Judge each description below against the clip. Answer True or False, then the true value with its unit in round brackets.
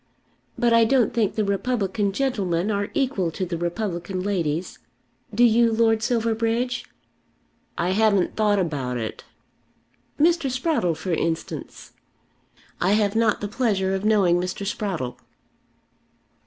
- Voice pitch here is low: False (205 Hz)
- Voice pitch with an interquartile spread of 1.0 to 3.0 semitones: False (4.0 semitones)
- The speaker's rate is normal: False (130 wpm)